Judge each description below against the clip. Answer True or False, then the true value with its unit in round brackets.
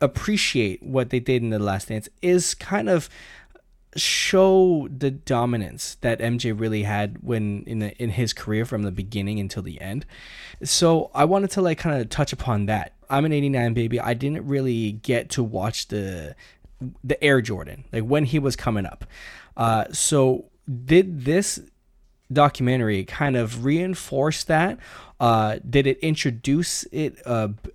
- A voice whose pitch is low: True (125 Hz)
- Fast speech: False (160 wpm)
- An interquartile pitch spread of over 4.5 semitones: True (5.2 semitones)